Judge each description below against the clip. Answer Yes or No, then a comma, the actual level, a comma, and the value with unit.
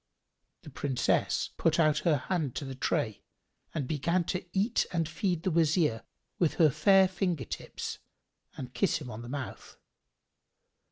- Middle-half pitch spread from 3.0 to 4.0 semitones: No, average, 4.8 semitones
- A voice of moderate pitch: Yes, medium, 155 Hz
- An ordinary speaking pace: Yes, average, 155 wpm